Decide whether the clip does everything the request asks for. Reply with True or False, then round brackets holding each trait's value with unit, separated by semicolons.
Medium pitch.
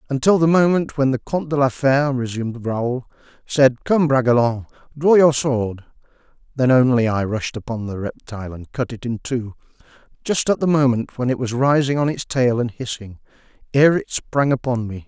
False (130 Hz)